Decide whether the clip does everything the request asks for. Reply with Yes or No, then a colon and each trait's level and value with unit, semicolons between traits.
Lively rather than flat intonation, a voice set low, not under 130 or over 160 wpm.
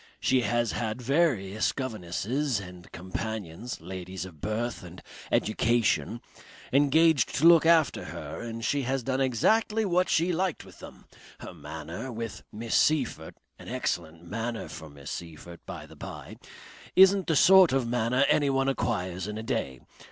Yes: wide, 6.8 semitones; low, 115 Hz; average, 150 wpm